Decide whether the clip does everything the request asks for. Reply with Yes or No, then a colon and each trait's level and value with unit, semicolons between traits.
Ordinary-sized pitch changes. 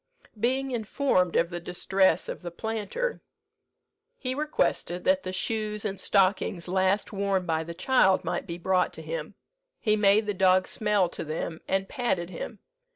Yes: average, 3.5 semitones